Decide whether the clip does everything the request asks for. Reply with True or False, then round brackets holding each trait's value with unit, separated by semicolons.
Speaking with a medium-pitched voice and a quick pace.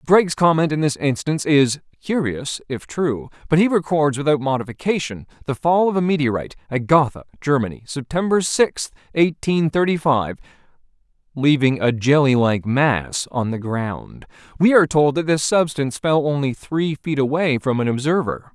False (145 Hz; 160 wpm)